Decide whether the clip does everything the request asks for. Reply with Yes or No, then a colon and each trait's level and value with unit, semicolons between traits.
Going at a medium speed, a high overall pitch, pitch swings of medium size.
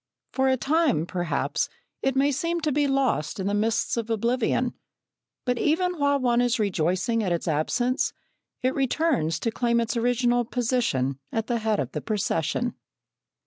Yes: average, 165 wpm; high, 240 Hz; average, 4.1 semitones